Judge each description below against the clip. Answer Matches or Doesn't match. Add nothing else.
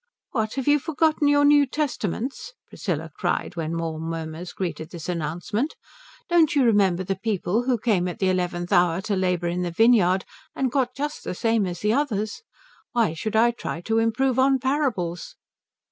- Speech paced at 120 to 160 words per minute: Doesn't match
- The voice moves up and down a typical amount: Doesn't match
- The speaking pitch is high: Matches